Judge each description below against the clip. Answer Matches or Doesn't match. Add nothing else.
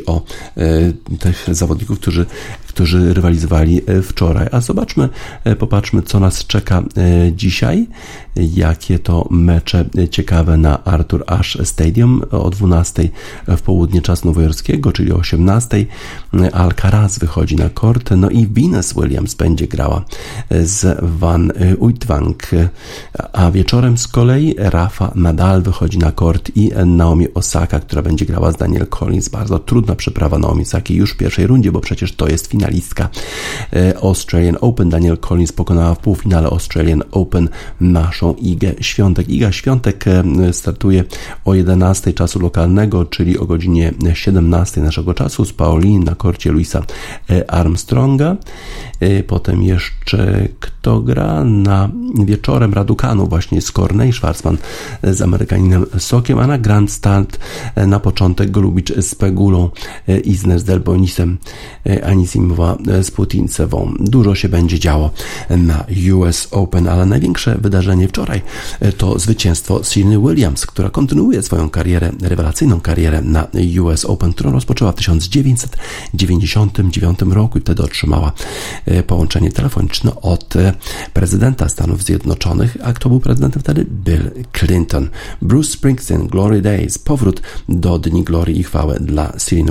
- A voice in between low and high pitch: Doesn't match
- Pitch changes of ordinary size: Matches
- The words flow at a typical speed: Matches